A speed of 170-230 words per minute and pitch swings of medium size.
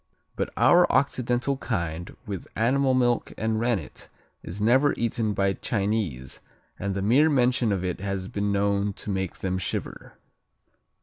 No: average, 145 wpm; average, 4.0 semitones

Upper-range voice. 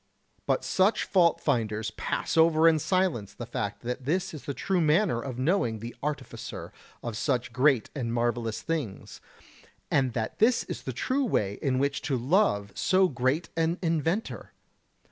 No: medium, 140 Hz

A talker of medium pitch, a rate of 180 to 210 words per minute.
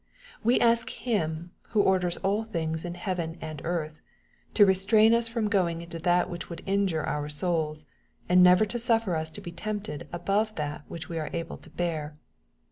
Yes: medium, 175 Hz; average, 185 wpm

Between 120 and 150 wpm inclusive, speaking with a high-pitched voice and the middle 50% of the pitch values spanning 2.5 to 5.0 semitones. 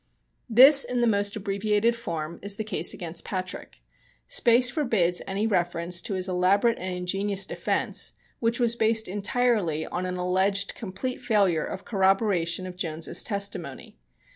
Yes: average, 145 wpm; high, 195 Hz; average, 3.8 semitones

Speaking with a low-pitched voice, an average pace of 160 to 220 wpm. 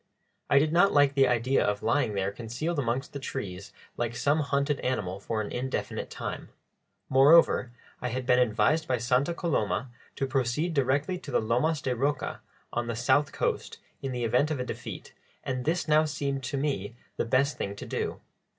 Yes: low, 130 Hz; average, 185 wpm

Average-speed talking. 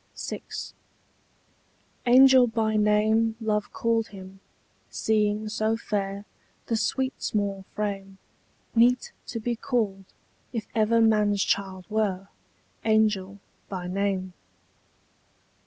No: slow, 100 wpm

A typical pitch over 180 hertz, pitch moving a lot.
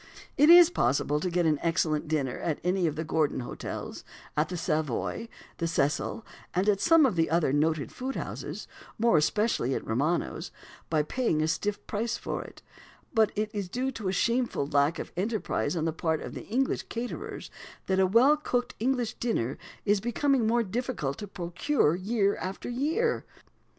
Yes: high, 190 Hz; wide, 7.0 semitones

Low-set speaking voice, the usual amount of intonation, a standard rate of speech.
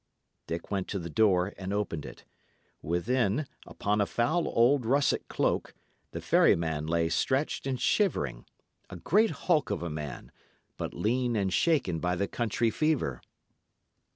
No: low, 100 Hz; wide, 7.4 semitones; average, 150 wpm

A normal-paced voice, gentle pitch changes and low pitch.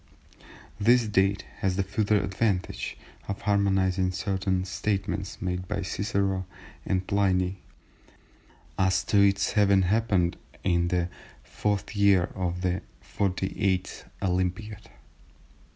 No: slow, 105 wpm; narrow, 1.6 semitones; very low, 95 Hz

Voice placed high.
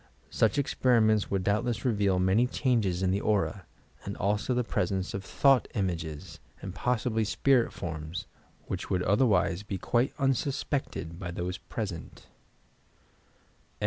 No: low, 100 Hz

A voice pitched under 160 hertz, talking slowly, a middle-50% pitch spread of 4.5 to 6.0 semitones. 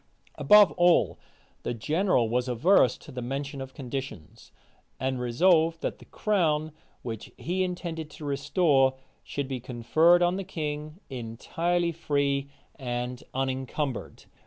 Yes: medium, 140 Hz; slow, 130 wpm; average, 4.8 semitones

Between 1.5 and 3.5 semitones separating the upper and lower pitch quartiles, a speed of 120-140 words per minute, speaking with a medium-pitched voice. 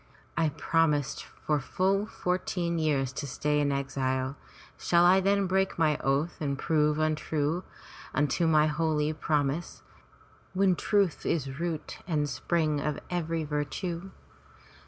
Yes: average, 2.9 semitones; slow, 135 wpm; medium, 155 Hz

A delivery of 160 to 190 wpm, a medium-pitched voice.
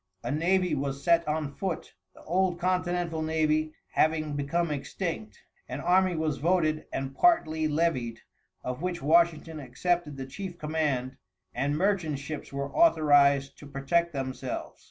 No: average, 140 wpm; medium, 155 Hz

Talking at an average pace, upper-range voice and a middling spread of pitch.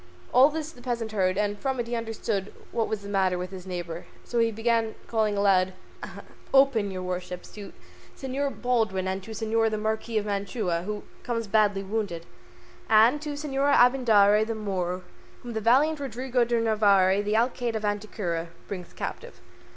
Yes: average, 180 wpm; high, 215 Hz; average, 3.5 semitones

